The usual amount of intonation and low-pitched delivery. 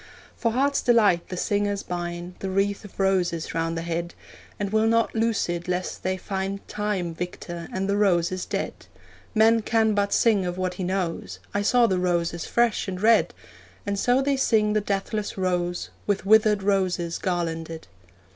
No: average, 3.2 semitones; high, 195 Hz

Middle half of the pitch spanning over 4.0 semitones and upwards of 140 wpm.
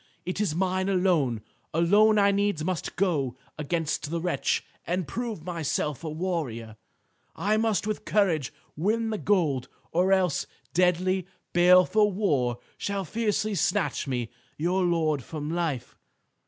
No: average, 4.4 semitones; slow, 135 wpm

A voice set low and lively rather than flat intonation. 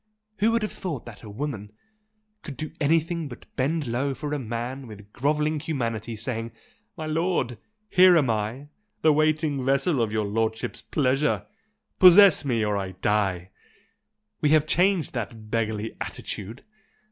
Yes: low, 130 Hz; wide, 5.7 semitones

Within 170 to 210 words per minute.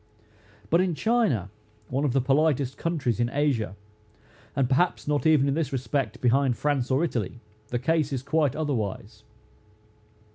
No: average, 150 wpm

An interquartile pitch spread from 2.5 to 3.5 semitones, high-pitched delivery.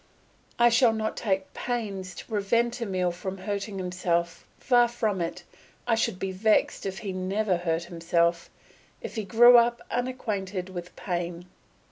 No: average, 4.2 semitones; high, 195 Hz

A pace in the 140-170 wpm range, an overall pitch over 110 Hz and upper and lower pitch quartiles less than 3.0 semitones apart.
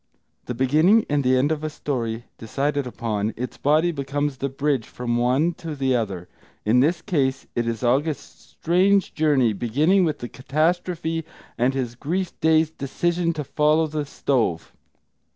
No: average, 160 wpm; medium, 140 Hz; average, 4.3 semitones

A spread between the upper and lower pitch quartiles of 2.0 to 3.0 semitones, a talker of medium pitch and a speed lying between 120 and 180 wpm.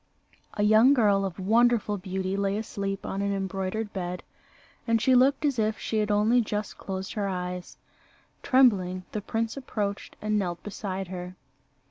No: average, 2.7 semitones; high, 205 Hz; average, 160 wpm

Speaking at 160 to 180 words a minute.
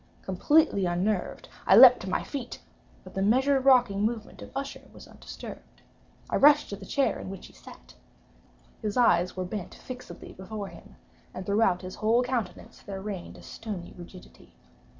Yes: average, 170 wpm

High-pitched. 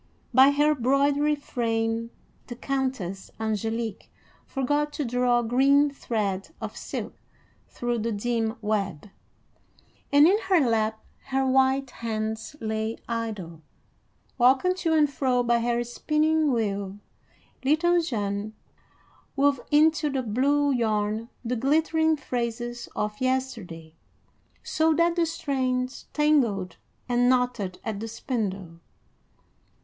Yes: high, 245 Hz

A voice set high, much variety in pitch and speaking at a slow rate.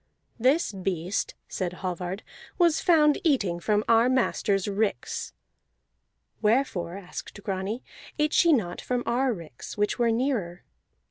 Yes: high, 210 Hz; wide, 5.8 semitones; slow, 125 wpm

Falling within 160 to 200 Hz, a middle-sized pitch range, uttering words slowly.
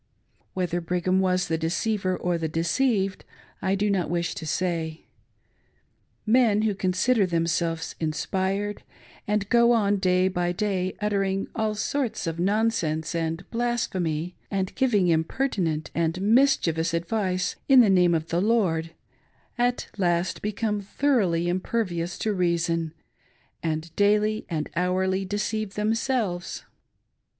Yes: medium, 185 Hz; average, 3.8 semitones; slow, 125 wpm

